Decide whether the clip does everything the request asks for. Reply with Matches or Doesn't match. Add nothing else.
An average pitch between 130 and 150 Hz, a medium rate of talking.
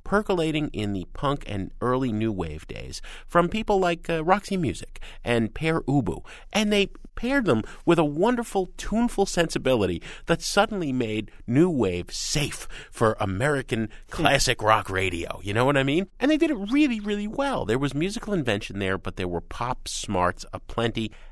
Matches